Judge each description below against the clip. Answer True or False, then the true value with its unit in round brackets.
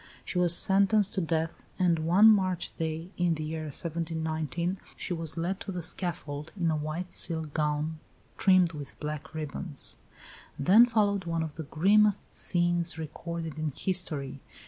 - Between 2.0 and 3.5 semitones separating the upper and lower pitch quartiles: True (2.7 semitones)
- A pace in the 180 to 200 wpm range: False (155 wpm)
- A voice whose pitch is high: False (165 Hz)